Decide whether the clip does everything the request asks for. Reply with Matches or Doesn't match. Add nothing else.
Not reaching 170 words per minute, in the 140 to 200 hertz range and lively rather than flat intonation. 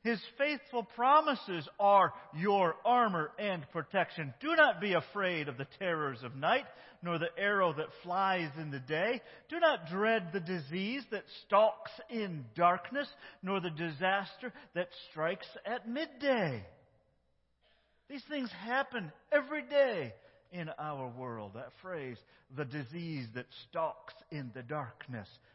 Matches